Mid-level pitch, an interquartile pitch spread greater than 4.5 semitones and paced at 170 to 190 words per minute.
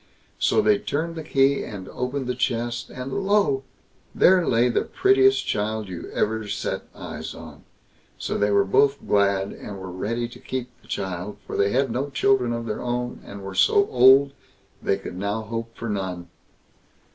No: low, 120 Hz; average, 5.1 semitones; average, 180 wpm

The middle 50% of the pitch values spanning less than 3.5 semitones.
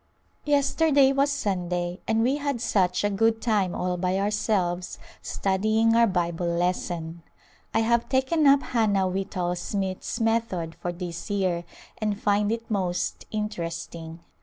No: average, 4.2 semitones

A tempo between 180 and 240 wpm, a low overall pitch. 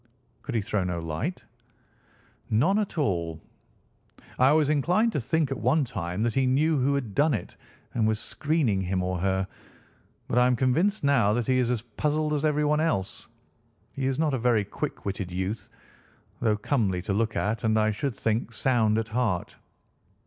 Yes: average, 185 wpm; low, 120 Hz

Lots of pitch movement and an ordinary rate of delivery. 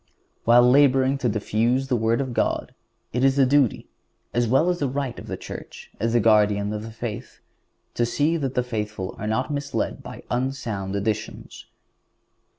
No: average, 3.6 semitones; average, 170 wpm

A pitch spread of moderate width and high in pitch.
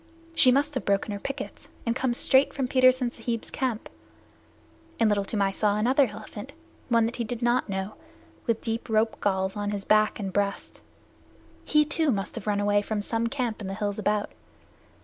Yes: average, 3.6 semitones; high, 225 Hz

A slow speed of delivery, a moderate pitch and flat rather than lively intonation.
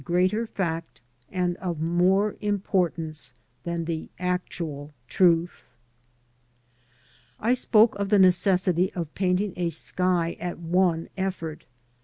Yes: slow, 110 wpm; medium, 180 Hz; narrow, 2.2 semitones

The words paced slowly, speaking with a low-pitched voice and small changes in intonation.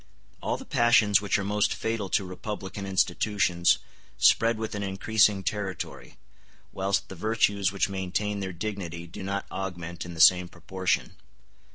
No: average, 155 wpm; low, 100 Hz; narrow, 2.2 semitones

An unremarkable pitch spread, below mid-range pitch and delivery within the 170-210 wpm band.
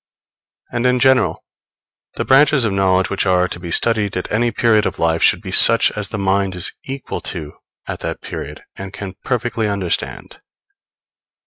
Yes: average, 4.2 semitones; low, 100 Hz; average, 175 wpm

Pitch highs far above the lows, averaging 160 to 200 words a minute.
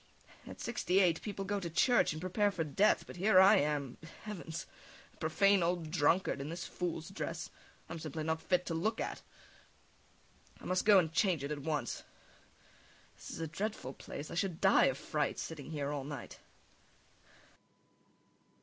No: average, 3.8 semitones; average, 170 wpm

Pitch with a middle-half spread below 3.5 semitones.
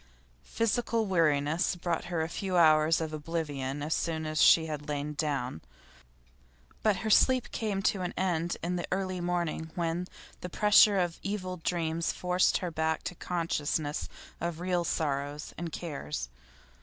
Yes: average, 2.8 semitones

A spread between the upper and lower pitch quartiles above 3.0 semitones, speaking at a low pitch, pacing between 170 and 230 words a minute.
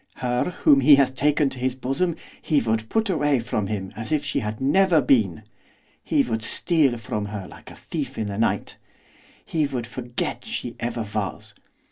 Yes: average, 4.6 semitones; low, 125 Hz; average, 185 wpm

